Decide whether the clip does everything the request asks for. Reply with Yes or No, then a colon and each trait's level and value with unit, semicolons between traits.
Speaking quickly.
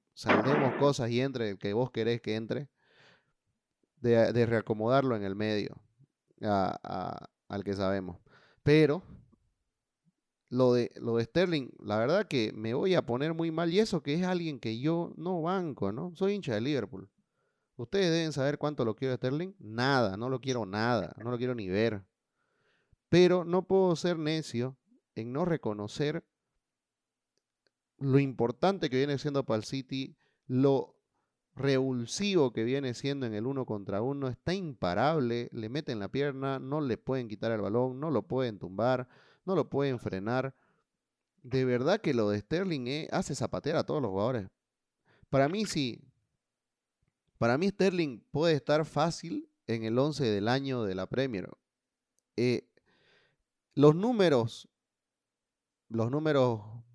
No: average, 155 wpm